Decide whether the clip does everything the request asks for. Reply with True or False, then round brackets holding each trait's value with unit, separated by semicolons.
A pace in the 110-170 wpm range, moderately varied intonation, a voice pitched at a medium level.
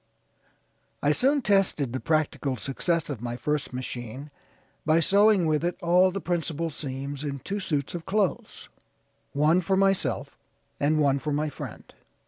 True (150 wpm; 4.4 semitones; 155 Hz)